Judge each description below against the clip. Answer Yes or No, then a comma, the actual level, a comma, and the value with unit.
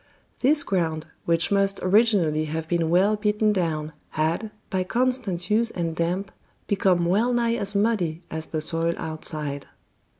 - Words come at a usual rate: Yes, average, 145 wpm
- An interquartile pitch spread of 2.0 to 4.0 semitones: No, average, 4.4 semitones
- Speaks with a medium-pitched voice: Yes, medium, 180 Hz